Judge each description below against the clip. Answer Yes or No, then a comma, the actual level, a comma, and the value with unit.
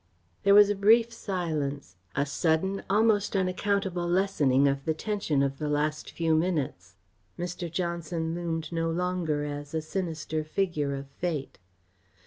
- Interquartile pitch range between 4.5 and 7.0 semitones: No, average, 4.1 semitones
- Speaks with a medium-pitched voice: Yes, medium, 165 Hz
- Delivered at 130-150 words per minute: Yes, average, 140 wpm